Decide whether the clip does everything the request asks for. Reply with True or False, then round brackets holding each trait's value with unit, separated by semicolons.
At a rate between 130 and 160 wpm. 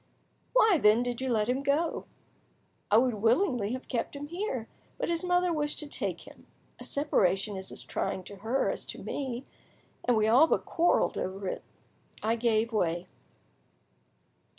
False (170 wpm)